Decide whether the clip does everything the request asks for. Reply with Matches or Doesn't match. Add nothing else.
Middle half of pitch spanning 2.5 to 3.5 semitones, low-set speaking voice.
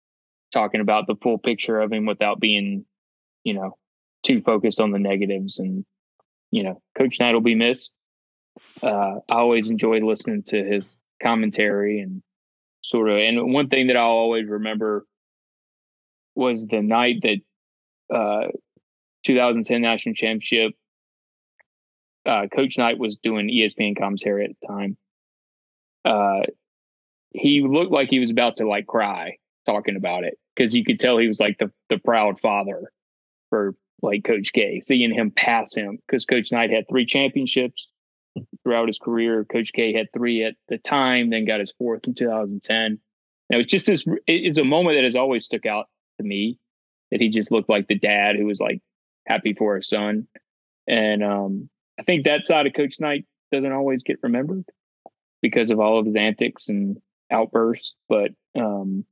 Matches